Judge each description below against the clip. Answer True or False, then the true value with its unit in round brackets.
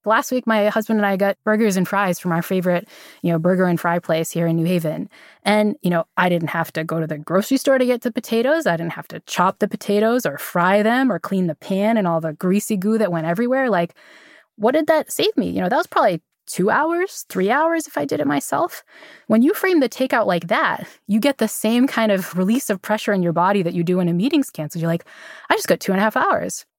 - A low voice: False (205 Hz)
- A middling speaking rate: False (260 wpm)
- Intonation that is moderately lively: False (5.8 semitones)